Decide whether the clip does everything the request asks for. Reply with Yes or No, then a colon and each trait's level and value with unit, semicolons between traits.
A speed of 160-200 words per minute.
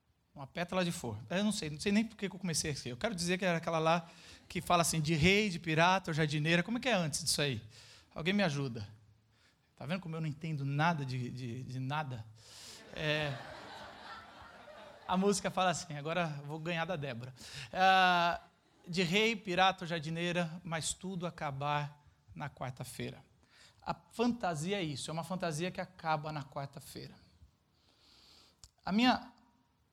Yes: average, 170 wpm